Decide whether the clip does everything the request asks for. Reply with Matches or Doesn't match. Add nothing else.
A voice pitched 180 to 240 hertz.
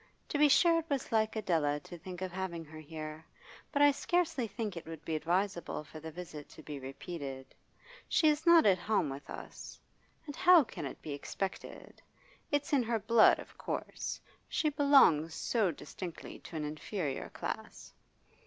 Matches